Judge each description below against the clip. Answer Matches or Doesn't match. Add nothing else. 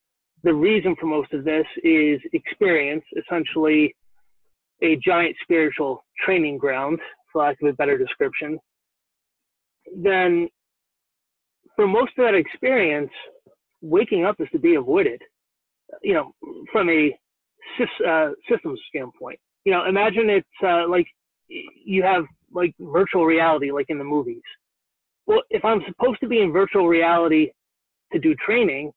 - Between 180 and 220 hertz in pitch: Matches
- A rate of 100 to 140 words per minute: Matches